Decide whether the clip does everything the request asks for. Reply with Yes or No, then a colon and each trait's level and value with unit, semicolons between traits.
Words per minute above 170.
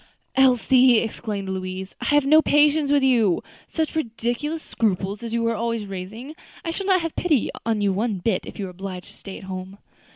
Yes: average, 190 wpm